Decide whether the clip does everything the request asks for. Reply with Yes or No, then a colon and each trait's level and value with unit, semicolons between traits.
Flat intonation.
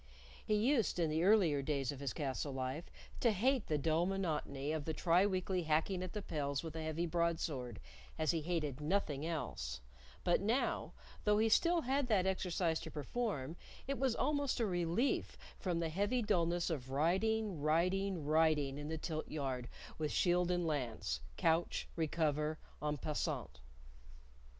No: average, 4.5 semitones